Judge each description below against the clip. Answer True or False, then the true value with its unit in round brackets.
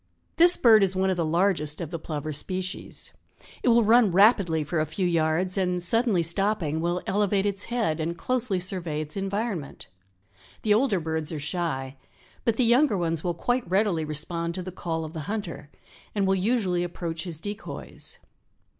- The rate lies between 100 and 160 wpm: False (180 wpm)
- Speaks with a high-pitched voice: False (180 Hz)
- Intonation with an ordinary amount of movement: True (4.1 semitones)